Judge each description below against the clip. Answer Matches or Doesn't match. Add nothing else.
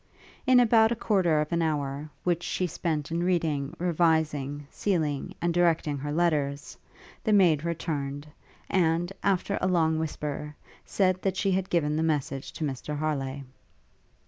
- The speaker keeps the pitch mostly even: Doesn't match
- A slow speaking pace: Doesn't match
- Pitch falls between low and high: Matches